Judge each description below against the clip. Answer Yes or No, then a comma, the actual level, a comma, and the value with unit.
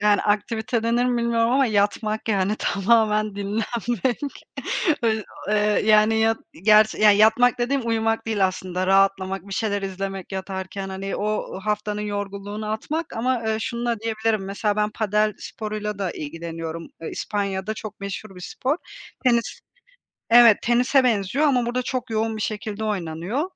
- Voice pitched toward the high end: Yes, high, 215 Hz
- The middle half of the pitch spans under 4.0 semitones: Yes, narrow, 2.6 semitones